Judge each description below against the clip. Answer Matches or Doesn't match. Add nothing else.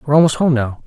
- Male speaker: Matches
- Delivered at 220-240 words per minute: Doesn't match